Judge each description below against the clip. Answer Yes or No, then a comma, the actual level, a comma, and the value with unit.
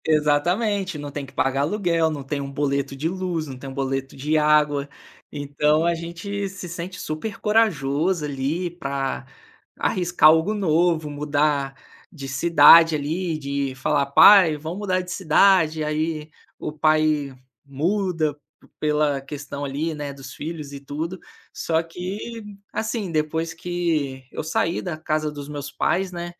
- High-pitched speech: No, medium, 155 Hz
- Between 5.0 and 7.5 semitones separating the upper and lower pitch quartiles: No, average, 3.4 semitones